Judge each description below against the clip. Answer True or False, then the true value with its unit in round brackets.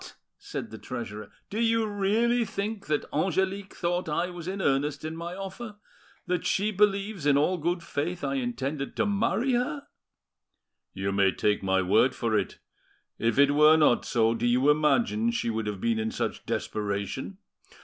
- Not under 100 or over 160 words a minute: False (170 wpm)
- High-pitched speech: False (160 Hz)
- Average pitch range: False (8.6 semitones)